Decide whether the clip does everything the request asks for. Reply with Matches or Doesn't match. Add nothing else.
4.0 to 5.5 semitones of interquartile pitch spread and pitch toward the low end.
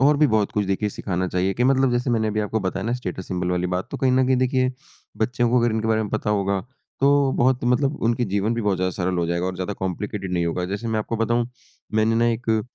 Matches